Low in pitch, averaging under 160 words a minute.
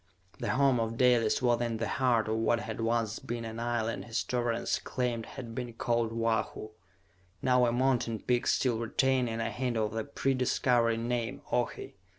No: low, 120 Hz; average, 170 wpm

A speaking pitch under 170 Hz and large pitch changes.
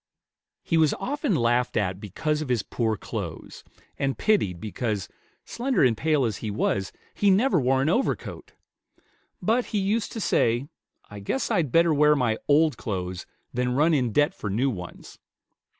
Yes: low, 135 Hz; wide, 6.9 semitones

